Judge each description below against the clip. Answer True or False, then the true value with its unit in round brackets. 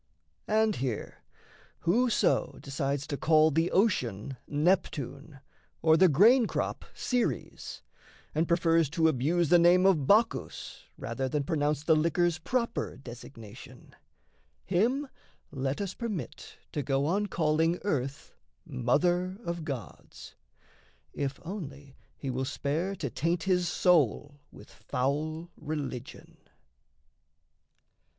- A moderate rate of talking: False (115 wpm)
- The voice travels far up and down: False (4.3 semitones)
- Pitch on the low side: False (160 Hz)